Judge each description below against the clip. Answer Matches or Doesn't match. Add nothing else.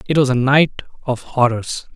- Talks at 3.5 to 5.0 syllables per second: Matches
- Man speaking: Matches